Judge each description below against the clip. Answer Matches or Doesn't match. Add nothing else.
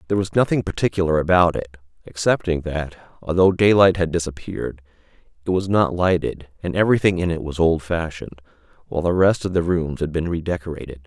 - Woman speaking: Doesn't match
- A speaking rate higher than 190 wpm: Doesn't match